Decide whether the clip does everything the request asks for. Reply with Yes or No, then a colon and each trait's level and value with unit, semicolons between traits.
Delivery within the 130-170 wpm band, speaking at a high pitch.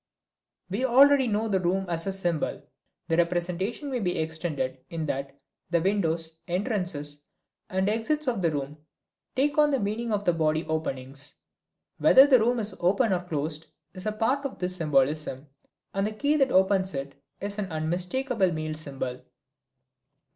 No: average, 160 wpm; medium, 180 Hz